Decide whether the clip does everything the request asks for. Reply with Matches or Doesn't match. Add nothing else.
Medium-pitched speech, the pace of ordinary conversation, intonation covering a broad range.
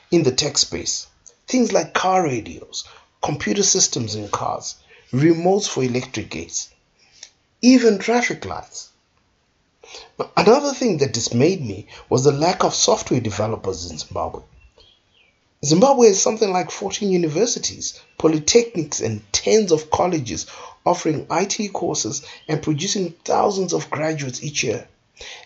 Doesn't match